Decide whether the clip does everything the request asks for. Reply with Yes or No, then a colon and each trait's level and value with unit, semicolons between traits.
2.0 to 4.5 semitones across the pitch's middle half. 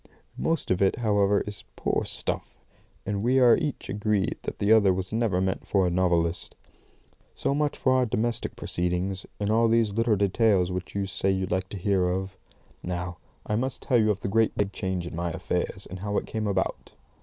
Yes: average, 3.3 semitones